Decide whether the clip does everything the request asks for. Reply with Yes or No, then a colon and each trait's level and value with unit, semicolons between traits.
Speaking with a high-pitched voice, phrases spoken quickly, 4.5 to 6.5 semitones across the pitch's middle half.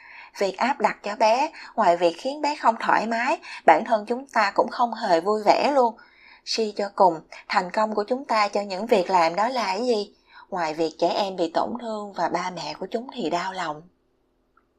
No: high, 210 Hz; average, 220 wpm; average, 4.9 semitones